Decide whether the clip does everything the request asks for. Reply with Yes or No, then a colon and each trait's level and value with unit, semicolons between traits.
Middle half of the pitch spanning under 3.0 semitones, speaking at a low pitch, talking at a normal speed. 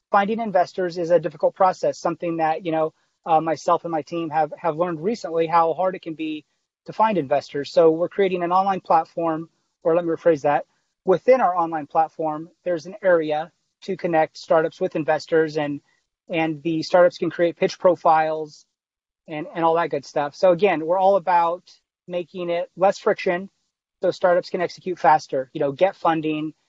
No: narrow, 2.5 semitones; medium, 170 Hz; average, 185 wpm